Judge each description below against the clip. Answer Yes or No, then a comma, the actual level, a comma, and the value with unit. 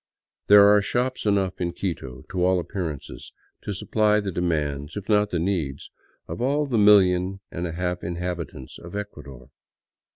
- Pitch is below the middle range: Yes, very low, 90 Hz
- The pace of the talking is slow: No, average, 160 wpm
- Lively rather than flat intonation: No, average, 3.6 semitones